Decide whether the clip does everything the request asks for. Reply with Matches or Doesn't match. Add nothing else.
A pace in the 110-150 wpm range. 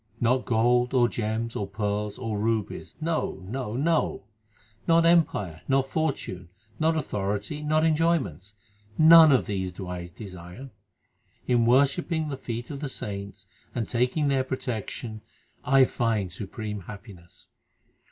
Matches